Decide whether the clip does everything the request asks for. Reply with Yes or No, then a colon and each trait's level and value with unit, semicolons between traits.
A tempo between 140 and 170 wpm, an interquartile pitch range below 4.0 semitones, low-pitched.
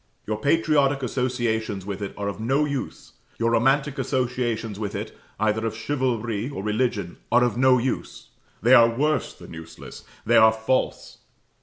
Yes: average, 160 wpm; average, 3.3 semitones; low, 120 Hz